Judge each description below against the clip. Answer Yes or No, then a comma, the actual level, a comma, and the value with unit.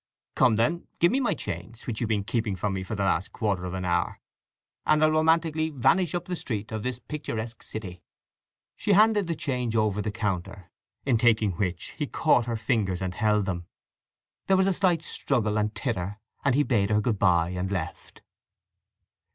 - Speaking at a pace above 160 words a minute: Yes, average, 190 wpm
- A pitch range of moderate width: No, wide, 7.0 semitones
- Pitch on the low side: Yes, low, 110 Hz